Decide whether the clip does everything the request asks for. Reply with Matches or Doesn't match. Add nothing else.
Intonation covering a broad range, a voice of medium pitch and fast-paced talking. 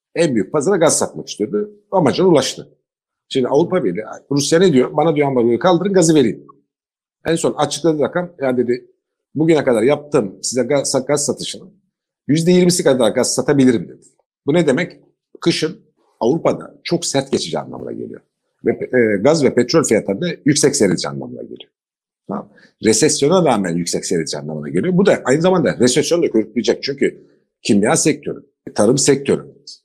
Matches